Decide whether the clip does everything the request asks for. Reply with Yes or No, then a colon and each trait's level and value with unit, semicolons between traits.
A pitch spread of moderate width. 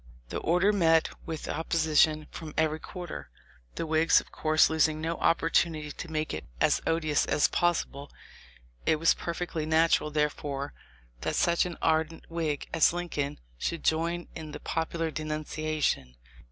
No: narrow, 1.4 semitones